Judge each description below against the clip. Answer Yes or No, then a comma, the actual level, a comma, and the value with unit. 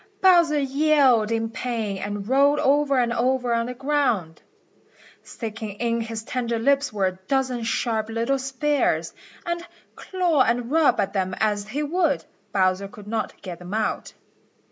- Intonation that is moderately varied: Yes, average, 4.7 semitones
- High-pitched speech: Yes, high, 235 Hz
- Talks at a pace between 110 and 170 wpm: Yes, average, 155 wpm